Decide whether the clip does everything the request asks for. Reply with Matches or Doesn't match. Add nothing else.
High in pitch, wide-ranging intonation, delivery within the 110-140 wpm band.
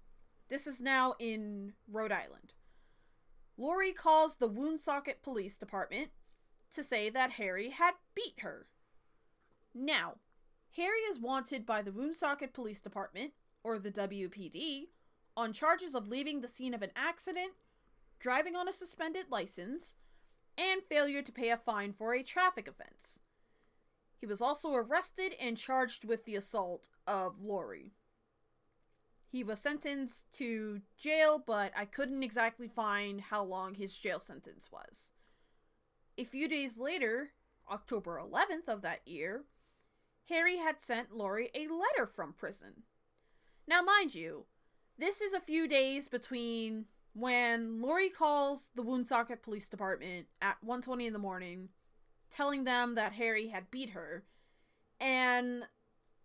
Matches